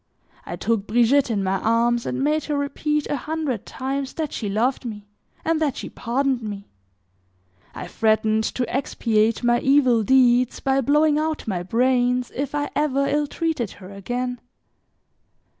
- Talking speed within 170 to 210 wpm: No, average, 160 wpm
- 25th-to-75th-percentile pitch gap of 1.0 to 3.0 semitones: No, average, 3.9 semitones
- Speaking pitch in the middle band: No, very high, 250 Hz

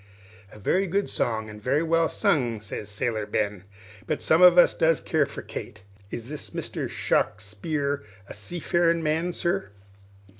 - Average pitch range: No, wide, 7.8 semitones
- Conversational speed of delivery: Yes, average, 155 wpm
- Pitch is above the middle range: No, medium, 145 Hz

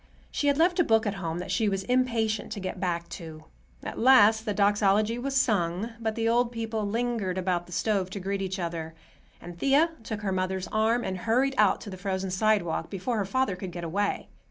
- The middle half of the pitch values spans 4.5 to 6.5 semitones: No, average, 3.7 semitones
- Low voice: No, high, 205 Hz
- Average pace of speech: No, fast, 215 wpm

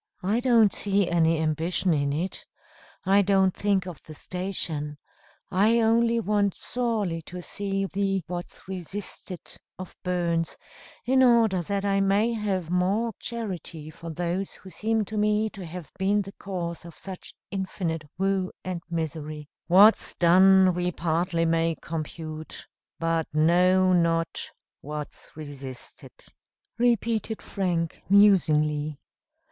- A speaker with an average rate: No, slow, 130 wpm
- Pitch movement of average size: Yes, average, 3.3 semitones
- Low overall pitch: No, medium, 185 Hz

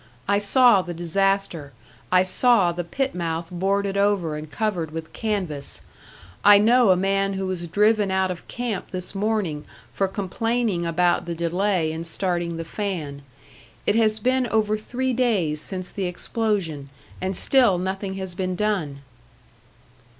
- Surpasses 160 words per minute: No, average, 150 wpm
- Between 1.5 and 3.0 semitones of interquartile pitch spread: No, average, 3.6 semitones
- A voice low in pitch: No, high, 190 Hz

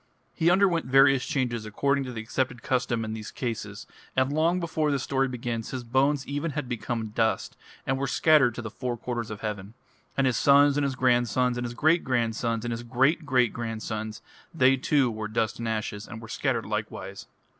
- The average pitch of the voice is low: Yes, low, 125 Hz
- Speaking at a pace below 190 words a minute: No, average, 200 wpm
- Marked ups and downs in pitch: No, average, 3.4 semitones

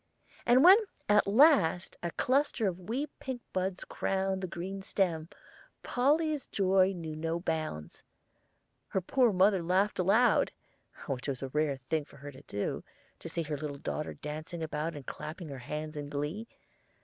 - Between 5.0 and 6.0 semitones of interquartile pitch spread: Yes, average, 5.3 semitones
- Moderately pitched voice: Yes, medium, 175 Hz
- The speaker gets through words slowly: No, average, 160 wpm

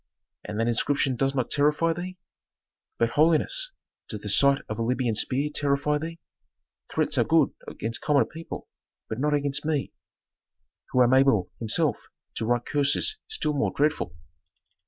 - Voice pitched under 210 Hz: Yes, medium, 140 Hz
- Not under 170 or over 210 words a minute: No, average, 155 wpm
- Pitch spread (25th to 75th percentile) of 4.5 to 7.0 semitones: No, average, 3.7 semitones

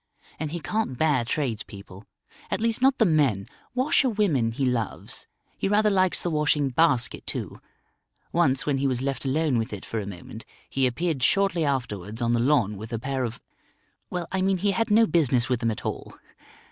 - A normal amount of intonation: No, wide, 7.0 semitones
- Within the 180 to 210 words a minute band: Yes, average, 195 wpm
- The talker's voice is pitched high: No, low, 135 Hz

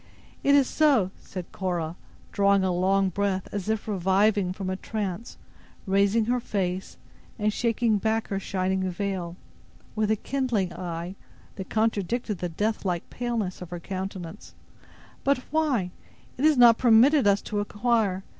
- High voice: Yes, high, 200 Hz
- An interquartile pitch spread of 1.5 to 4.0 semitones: Yes, average, 3.3 semitones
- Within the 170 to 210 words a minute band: No, average, 145 wpm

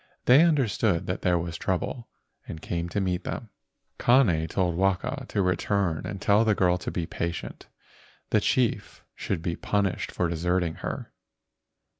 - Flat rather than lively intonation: No, average, 3.2 semitones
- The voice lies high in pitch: No, very low, 90 Hz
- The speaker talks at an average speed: Yes, average, 155 wpm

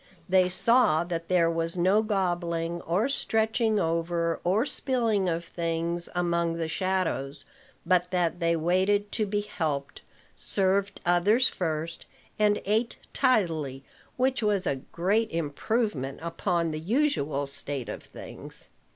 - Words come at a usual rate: No, slow, 130 wpm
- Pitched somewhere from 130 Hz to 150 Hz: No, medium, 175 Hz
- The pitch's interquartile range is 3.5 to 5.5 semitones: Yes, average, 3.8 semitones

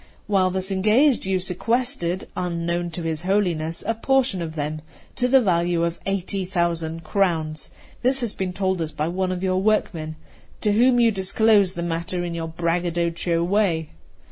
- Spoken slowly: No, average, 170 wpm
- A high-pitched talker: No, medium, 180 Hz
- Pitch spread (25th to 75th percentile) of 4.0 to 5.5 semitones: No, average, 3.2 semitones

